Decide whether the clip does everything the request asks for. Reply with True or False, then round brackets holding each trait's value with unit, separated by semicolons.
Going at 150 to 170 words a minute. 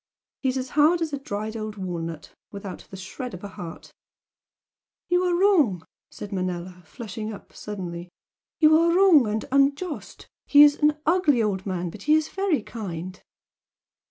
True (165 wpm)